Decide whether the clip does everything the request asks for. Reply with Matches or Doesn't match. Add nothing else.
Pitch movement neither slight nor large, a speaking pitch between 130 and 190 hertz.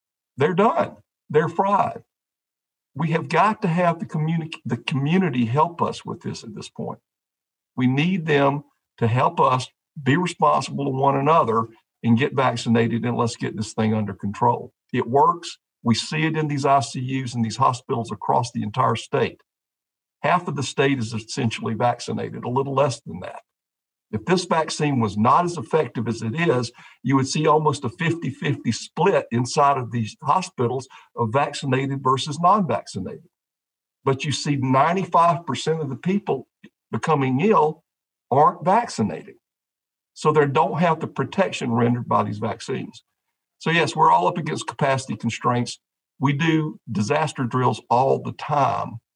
Matches